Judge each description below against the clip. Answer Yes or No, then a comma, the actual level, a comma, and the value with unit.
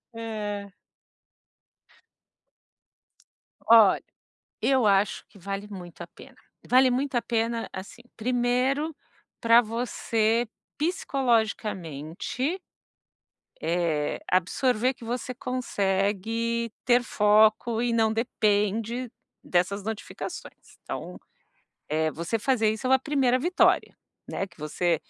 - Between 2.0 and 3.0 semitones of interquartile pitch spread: No, average, 3.7 semitones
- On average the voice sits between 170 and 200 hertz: No, high, 225 Hz